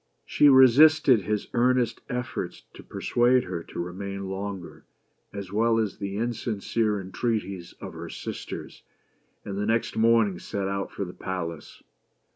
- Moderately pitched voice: No, low, 105 Hz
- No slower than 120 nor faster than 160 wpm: Yes, average, 140 wpm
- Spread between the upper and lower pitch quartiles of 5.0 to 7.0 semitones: No, average, 3.5 semitones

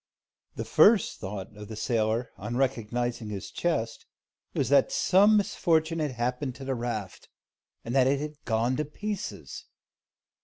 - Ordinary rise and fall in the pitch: No, wide, 5.9 semitones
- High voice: No, low, 125 Hz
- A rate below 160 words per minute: Yes, average, 150 wpm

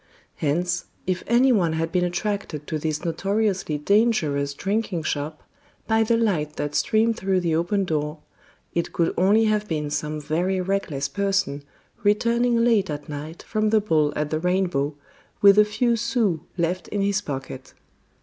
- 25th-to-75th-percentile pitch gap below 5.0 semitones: No, wide, 5.5 semitones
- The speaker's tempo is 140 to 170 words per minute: Yes, average, 160 wpm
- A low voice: No, medium, 180 Hz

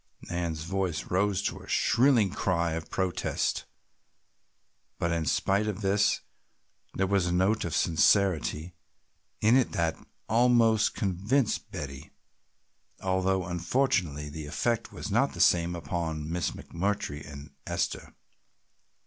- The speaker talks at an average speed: No, slow, 125 wpm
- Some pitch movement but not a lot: Yes, average, 3.9 semitones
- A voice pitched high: No, very low, 90 Hz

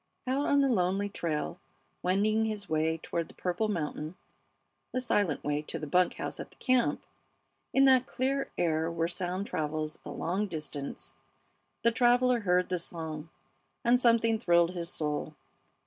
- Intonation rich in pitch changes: Yes, wide, 6.2 semitones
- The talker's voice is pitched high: No, medium, 180 Hz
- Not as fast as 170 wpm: Yes, average, 160 wpm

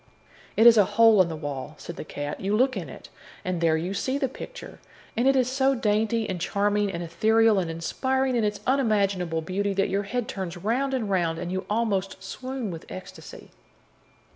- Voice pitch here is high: Yes, high, 205 Hz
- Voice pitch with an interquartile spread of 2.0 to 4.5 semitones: No, average, 4.9 semitones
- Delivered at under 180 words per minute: No, average, 200 wpm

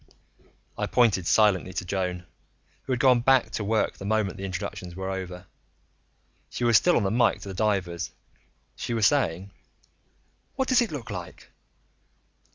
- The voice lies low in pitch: Yes, low, 100 Hz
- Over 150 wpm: Yes, average, 165 wpm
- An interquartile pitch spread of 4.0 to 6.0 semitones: Yes, average, 4.3 semitones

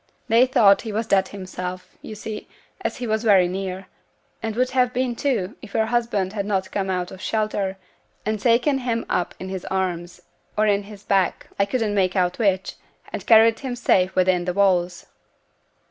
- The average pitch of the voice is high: Yes, high, 200 Hz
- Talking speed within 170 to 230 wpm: Yes, average, 190 wpm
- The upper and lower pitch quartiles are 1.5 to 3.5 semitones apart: Yes, average, 3.2 semitones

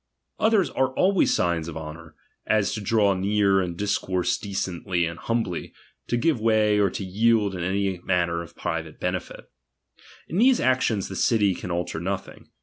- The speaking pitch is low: Yes, very low, 95 Hz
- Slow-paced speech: No, average, 170 wpm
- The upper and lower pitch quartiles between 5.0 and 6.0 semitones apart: No, average, 4.1 semitones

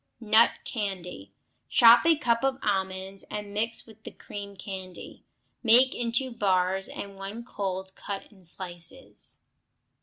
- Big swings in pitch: No, average, 3.5 semitones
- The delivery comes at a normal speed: No, slow, 130 wpm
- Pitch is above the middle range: Yes, high, 200 Hz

